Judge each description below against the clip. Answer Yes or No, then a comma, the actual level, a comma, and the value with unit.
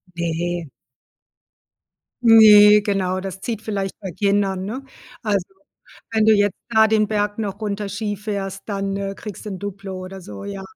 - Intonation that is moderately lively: No, narrow, 1.6 semitones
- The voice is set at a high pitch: Yes, high, 200 Hz